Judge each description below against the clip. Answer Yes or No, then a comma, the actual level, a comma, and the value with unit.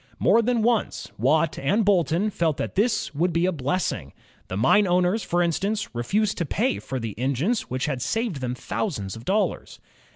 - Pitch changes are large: Yes, wide, 7.9 semitones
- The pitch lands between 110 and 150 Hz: No, medium, 175 Hz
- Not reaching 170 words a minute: No, average, 195 wpm